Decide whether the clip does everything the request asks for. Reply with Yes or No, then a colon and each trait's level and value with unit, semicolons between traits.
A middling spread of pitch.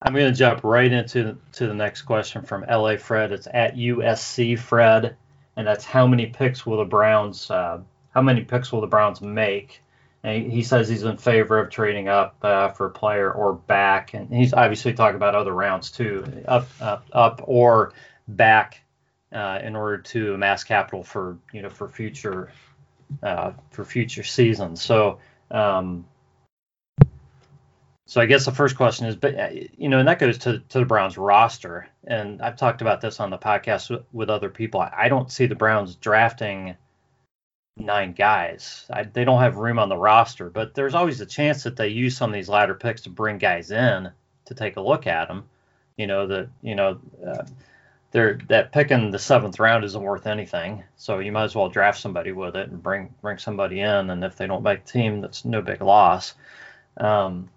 Yes: average, 3.3 semitones